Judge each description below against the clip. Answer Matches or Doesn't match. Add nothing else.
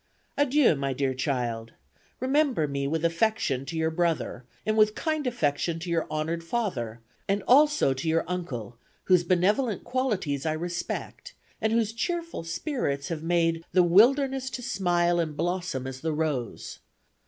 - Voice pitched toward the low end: Doesn't match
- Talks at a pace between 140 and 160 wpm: Matches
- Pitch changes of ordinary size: Doesn't match